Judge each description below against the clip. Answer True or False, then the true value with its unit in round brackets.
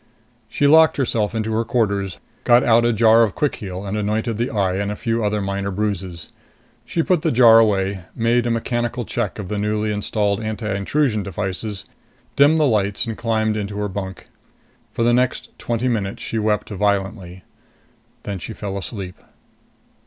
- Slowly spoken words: False (175 wpm)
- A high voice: False (105 Hz)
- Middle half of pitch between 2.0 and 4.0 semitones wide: True (2.8 semitones)